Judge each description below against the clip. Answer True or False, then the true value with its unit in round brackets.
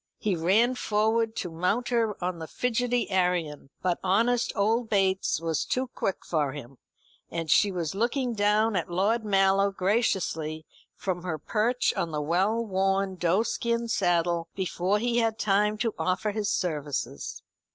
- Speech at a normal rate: True (150 wpm)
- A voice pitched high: True (195 Hz)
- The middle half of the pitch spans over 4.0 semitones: True (4.4 semitones)